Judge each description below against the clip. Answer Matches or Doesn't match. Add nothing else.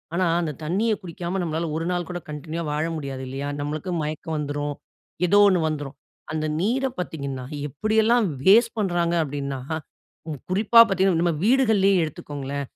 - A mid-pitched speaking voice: Matches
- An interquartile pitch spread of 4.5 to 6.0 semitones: Matches